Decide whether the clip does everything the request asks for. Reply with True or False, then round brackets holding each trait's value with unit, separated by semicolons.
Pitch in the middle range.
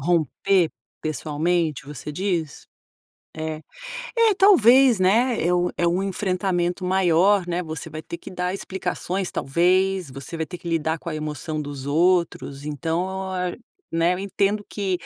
True (175 Hz)